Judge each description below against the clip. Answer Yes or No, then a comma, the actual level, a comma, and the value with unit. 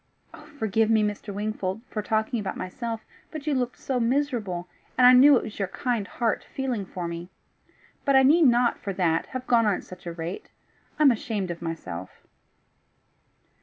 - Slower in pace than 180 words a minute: No, average, 185 wpm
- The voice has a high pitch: Yes, high, 220 Hz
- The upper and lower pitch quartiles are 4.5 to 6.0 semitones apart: Yes, average, 5.1 semitones